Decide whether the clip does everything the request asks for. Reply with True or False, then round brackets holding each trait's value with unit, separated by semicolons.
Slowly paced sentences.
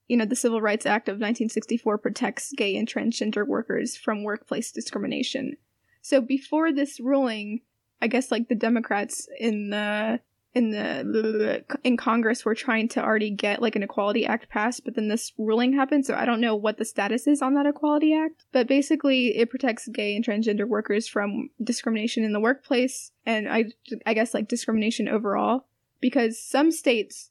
False (180 wpm)